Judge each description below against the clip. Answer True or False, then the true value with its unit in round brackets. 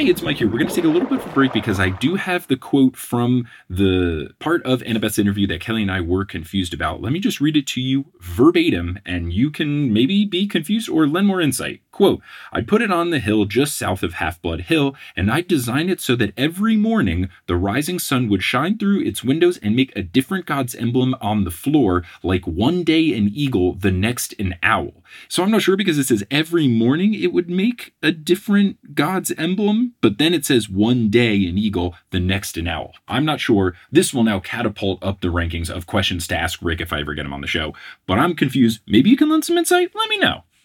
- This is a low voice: True (125 Hz)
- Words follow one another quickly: True (240 wpm)